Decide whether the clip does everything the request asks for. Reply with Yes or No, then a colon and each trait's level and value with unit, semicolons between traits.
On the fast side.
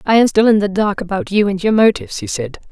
Yes: fast, 290 wpm